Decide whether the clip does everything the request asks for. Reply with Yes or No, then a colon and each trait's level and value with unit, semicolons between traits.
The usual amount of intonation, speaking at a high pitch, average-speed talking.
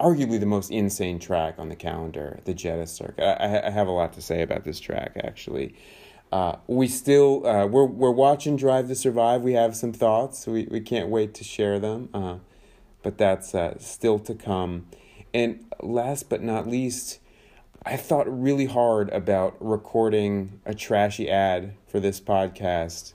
No: average, 4.4 semitones; low, 110 Hz; average, 175 wpm